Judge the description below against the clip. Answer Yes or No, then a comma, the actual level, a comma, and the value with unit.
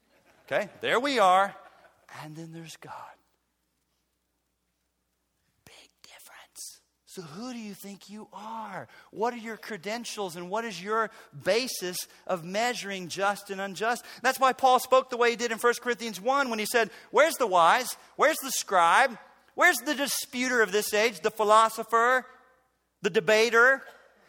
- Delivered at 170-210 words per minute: No, average, 155 wpm